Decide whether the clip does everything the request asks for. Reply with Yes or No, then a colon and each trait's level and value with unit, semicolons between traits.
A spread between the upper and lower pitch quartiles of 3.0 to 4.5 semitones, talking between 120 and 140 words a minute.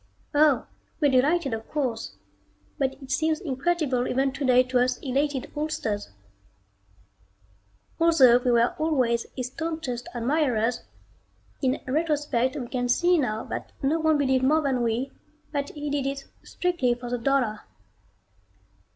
Yes: average, 3.4 semitones; slow, 135 wpm